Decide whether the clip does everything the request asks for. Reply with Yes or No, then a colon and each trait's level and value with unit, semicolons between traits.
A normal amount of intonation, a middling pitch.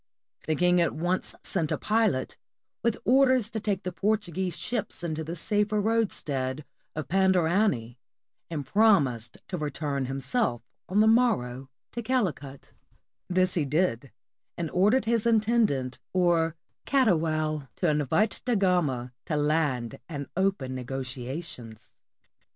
No: wide, 7.2 semitones; medium, 170 Hz